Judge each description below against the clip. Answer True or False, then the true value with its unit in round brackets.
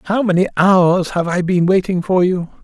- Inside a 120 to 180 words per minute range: False (205 wpm)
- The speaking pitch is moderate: True (180 Hz)